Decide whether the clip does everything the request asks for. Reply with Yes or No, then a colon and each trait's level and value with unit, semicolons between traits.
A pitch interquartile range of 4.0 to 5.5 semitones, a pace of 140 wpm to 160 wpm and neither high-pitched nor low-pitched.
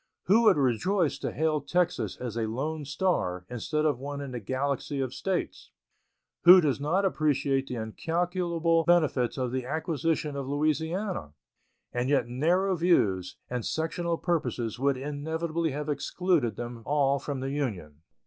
Yes: average, 4.7 semitones; average, 150 wpm; medium, 145 Hz